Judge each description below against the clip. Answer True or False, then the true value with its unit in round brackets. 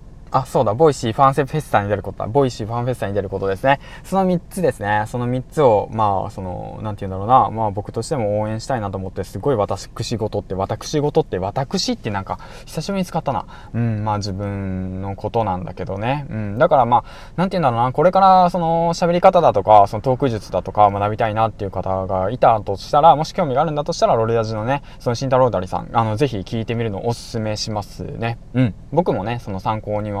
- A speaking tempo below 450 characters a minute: False (475 characters per minute)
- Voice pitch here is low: True (115 Hz)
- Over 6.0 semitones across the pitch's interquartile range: False (5.5 semitones)